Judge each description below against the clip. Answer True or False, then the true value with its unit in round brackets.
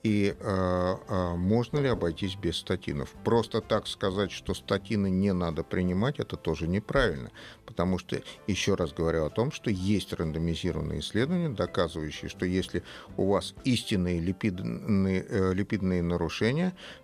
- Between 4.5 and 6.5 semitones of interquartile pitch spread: False (3.6 semitones)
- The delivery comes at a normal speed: True (135 wpm)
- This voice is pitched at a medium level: False (95 Hz)